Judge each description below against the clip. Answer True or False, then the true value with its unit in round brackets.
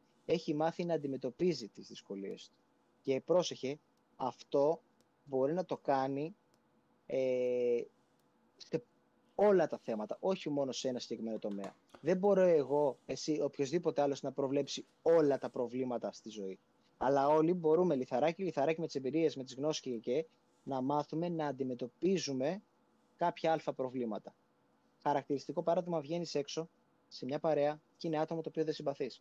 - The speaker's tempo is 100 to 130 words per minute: False (150 wpm)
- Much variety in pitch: False (3.7 semitones)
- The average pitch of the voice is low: False (145 Hz)